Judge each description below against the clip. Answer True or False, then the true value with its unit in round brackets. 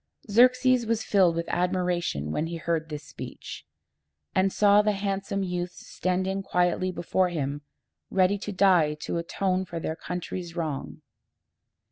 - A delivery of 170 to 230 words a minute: False (140 wpm)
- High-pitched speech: False (180 Hz)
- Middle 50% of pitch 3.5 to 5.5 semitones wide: False (2.7 semitones)